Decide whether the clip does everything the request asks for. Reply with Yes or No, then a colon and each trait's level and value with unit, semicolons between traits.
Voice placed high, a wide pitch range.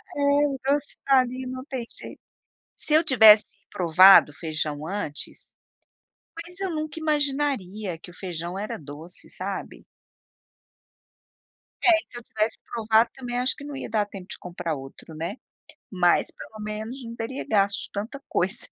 Yes: high, 220 Hz; wide, 6.8 semitones